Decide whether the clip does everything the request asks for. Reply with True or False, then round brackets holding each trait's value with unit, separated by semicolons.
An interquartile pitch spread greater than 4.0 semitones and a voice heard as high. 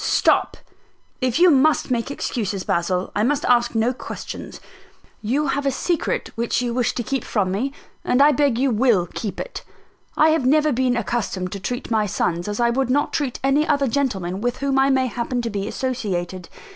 True (4.6 semitones; 245 Hz)